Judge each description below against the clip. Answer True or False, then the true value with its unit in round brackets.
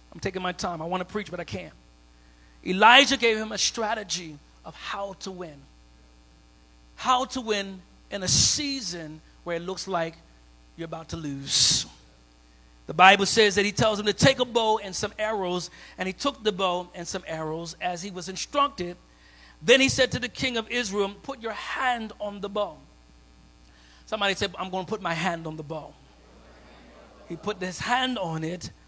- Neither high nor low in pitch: True (180 Hz)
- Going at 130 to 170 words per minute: False (190 wpm)